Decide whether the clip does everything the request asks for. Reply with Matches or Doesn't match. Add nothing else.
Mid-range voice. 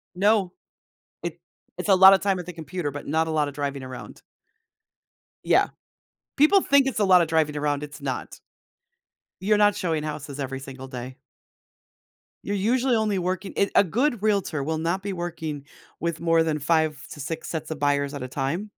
Matches